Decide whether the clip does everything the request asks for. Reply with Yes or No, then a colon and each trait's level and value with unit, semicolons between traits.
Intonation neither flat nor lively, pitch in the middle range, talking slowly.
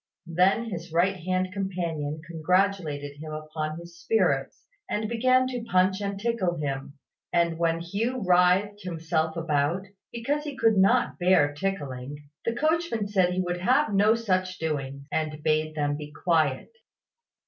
No: average, 4.5 semitones; medium, 180 Hz; average, 150 wpm